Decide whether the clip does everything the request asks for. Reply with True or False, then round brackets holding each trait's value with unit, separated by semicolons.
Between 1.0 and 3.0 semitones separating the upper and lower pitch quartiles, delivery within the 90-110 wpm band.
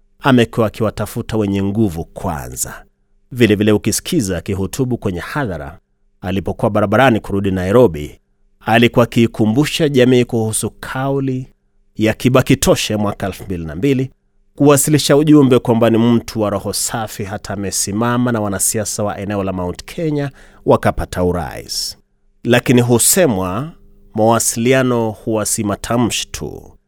False (3.8 semitones; 105 wpm)